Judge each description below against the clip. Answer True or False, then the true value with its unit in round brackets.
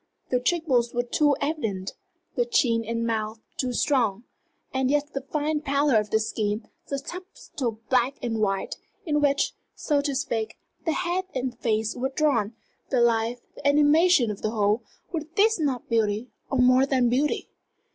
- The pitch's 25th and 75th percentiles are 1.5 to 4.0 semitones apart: False (4.5 semitones)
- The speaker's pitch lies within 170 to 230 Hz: False (255 Hz)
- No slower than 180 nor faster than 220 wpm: False (170 wpm)